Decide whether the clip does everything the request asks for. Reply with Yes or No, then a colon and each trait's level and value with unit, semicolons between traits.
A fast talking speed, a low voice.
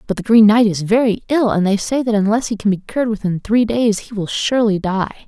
No: fast, 260 wpm; high, 215 Hz